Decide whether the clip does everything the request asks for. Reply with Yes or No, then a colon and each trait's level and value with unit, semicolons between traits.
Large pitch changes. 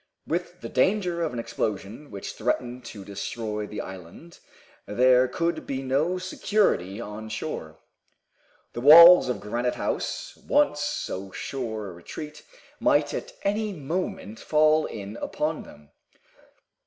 Yes: wide, 7.2 semitones